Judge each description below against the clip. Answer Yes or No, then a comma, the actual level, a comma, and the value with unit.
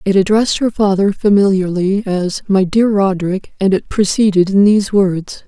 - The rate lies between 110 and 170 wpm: Yes, average, 165 wpm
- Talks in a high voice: Yes, high, 195 Hz